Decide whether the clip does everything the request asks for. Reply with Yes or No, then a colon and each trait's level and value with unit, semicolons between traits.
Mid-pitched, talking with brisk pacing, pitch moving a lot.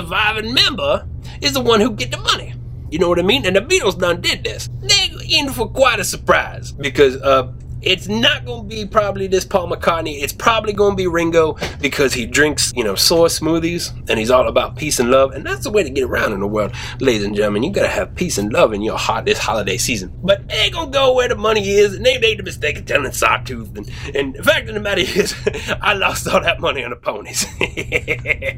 Yes: medium, 155 Hz; fast, 235 wpm; wide, 8.2 semitones